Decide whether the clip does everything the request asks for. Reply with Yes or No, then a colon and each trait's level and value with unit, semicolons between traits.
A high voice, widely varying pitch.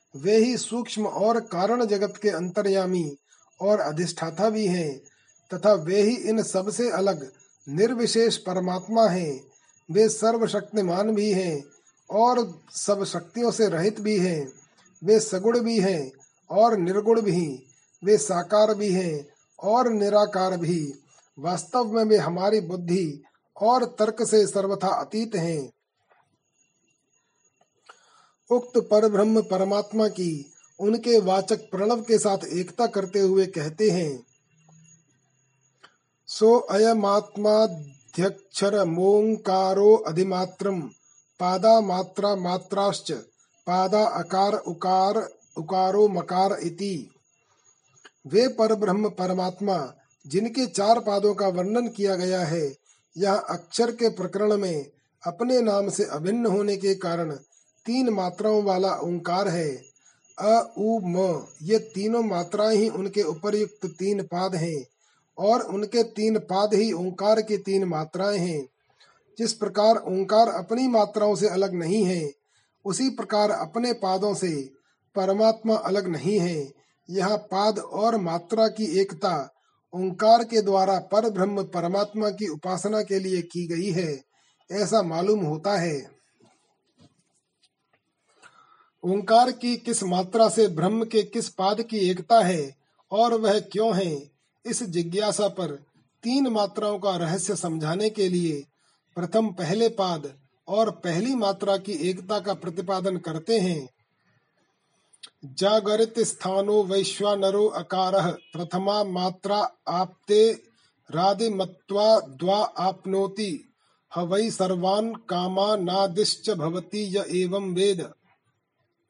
No: high, 195 Hz; average, 3.1 semitones